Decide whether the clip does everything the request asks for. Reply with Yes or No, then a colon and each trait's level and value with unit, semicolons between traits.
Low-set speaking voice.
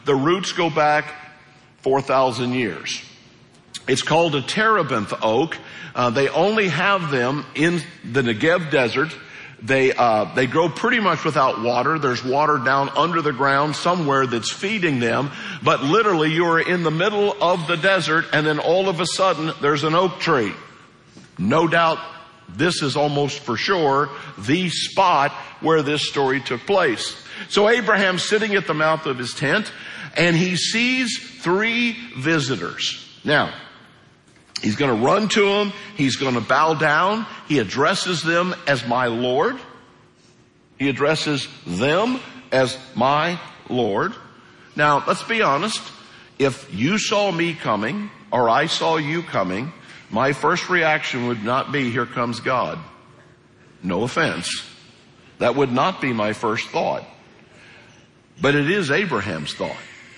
No: medium, 155 Hz